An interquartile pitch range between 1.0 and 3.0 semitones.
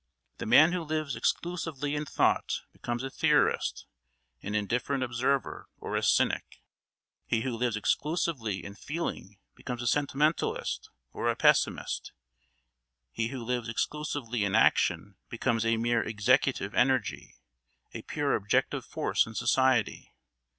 No: average, 4.4 semitones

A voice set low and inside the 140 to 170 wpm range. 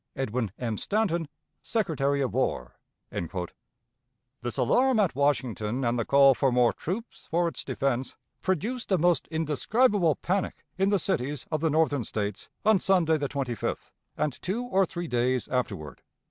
No: medium, 145 Hz; average, 150 wpm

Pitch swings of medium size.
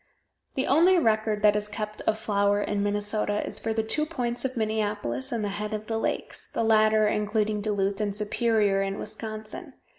No: narrow, 1.3 semitones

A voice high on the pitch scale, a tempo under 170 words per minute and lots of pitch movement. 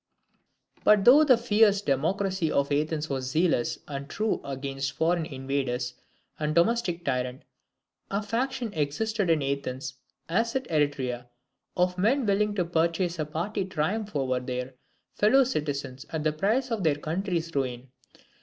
No: medium, 165 Hz; average, 145 wpm; wide, 6.9 semitones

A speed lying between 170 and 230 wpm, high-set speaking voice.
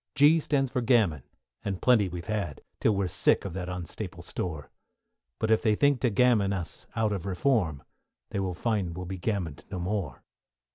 No: average, 190 wpm; low, 100 Hz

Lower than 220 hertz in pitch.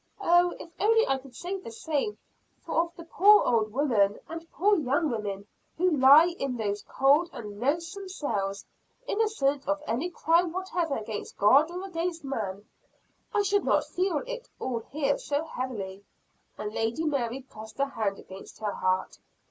No: very high, 285 Hz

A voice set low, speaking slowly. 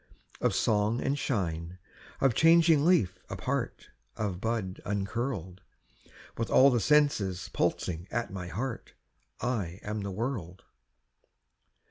Yes: low, 105 Hz; slow, 115 wpm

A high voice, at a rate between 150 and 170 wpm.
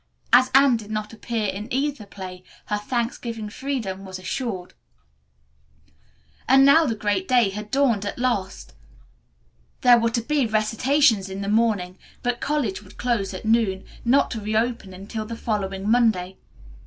Yes: high, 220 Hz; average, 155 wpm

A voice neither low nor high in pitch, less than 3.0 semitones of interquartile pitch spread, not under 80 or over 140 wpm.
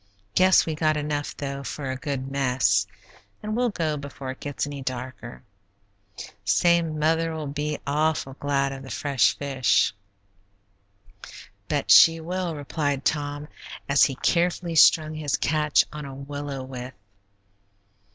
Yes: medium, 145 Hz; narrow, 2.5 semitones; slow, 135 wpm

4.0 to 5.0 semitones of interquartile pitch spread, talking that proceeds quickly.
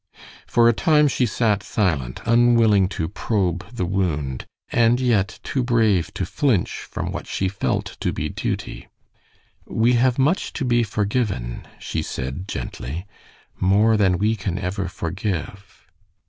No: average, 4.4 semitones; average, 145 wpm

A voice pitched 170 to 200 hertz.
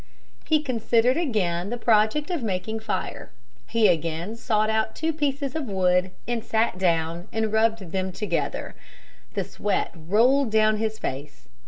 No: high, 220 Hz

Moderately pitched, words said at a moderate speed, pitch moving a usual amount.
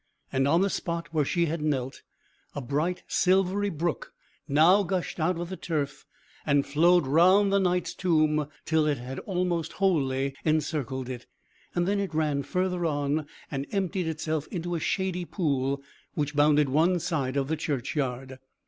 Yes: medium, 155 Hz; average, 160 wpm; average, 4.1 semitones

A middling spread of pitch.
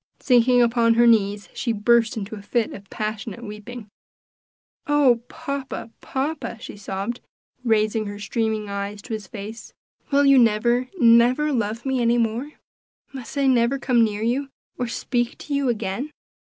Yes: average, 3.0 semitones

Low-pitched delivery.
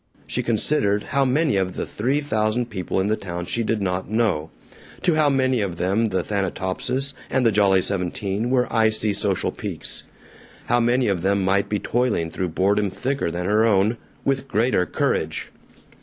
Yes: low, 105 Hz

